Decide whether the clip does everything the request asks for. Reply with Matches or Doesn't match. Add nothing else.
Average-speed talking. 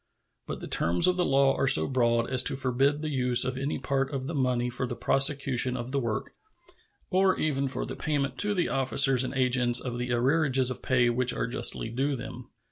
Doesn't match